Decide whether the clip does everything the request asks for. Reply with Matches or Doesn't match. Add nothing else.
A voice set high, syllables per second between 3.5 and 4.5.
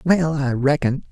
Doesn't match